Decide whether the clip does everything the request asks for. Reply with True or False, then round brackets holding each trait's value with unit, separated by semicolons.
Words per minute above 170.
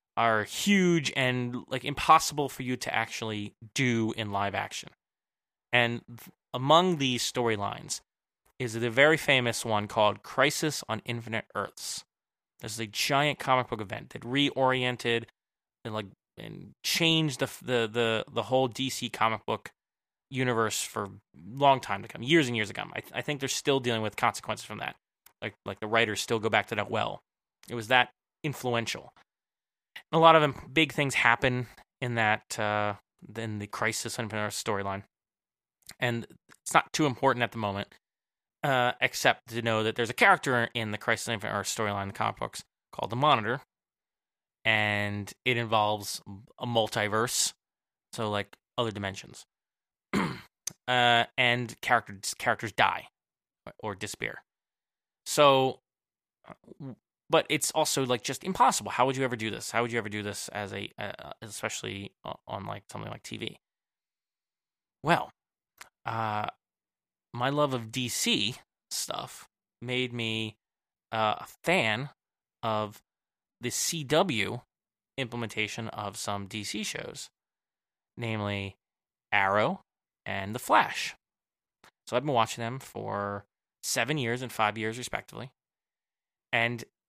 False (145 wpm)